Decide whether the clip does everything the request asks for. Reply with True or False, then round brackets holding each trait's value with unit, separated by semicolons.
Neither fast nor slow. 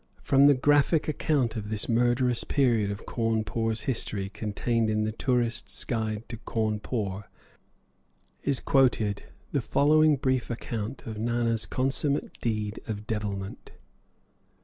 False (125 wpm)